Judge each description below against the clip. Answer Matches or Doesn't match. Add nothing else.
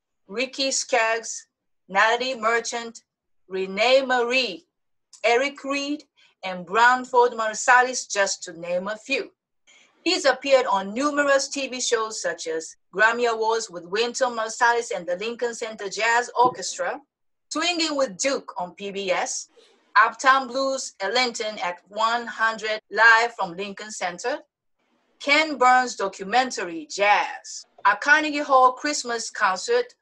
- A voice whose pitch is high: Matches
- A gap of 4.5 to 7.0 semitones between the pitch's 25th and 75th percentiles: Doesn't match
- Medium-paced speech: Doesn't match